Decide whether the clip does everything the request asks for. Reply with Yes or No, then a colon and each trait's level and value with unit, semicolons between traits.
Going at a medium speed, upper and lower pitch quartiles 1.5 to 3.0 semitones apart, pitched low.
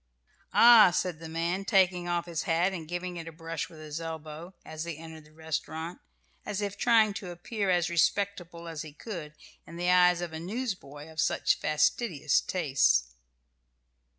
No: average, 175 wpm; narrow, 2.4 semitones; medium, 170 Hz